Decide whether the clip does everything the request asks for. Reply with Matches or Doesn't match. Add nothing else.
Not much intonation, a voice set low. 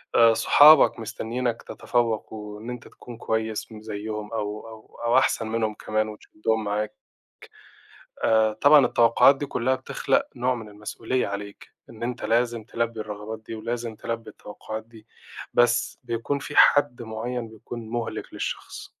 Matches